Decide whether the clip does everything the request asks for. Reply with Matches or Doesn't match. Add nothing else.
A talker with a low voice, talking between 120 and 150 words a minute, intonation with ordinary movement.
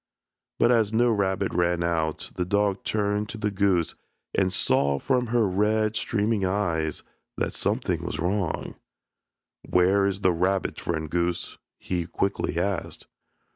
Matches